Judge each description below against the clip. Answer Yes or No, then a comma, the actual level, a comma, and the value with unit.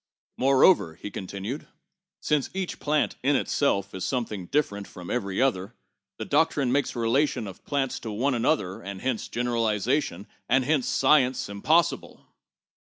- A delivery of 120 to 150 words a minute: Yes, average, 145 wpm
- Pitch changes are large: Yes, wide, 5.9 semitones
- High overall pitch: No, low, 125 Hz